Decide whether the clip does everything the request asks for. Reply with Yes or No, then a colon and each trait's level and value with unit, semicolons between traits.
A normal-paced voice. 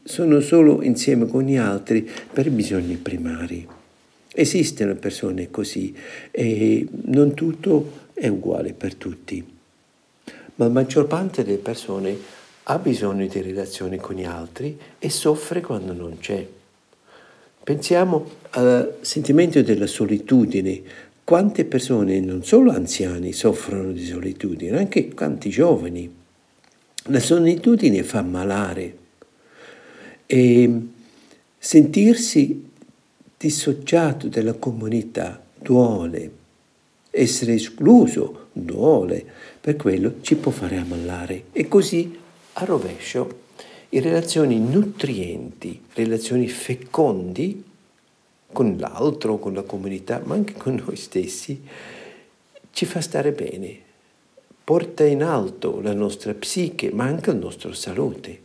No: slow, 110 wpm